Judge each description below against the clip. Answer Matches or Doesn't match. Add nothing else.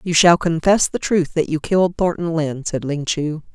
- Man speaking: Doesn't match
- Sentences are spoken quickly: Matches